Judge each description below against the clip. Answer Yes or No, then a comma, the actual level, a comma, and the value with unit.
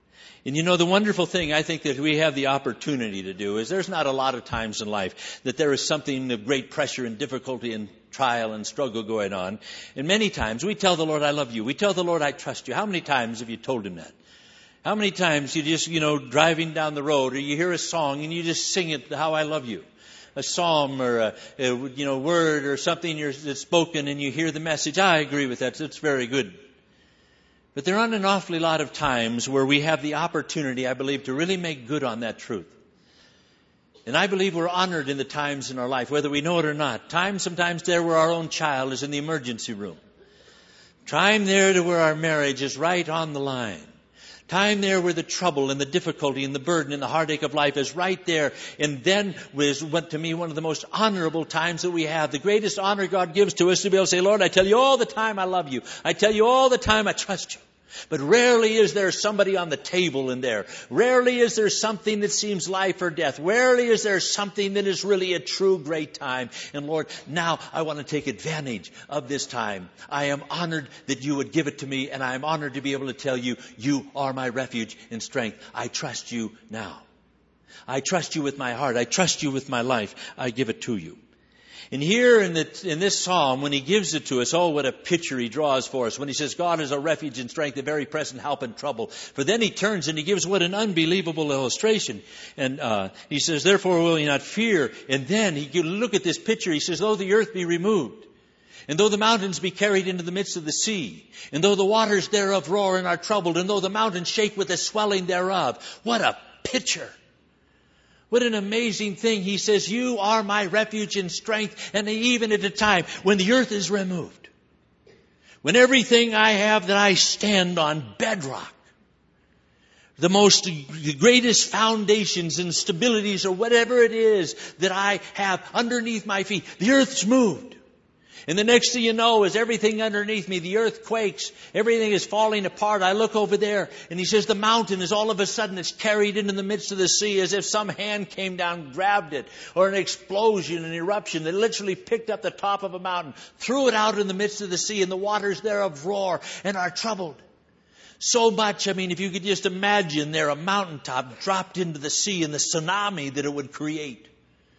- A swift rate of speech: Yes, fast, 225 wpm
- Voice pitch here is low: No, medium, 175 Hz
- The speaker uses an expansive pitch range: Yes, wide, 5.8 semitones